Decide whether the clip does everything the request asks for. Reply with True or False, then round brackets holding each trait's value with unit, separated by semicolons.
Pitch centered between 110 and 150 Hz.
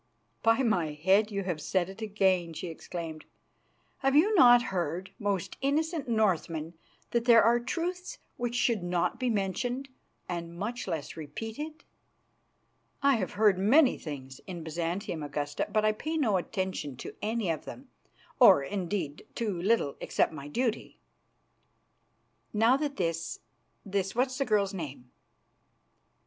False (200 Hz)